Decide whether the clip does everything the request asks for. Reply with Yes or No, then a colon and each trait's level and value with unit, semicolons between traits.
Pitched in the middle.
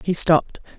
Yes: medium, 170 Hz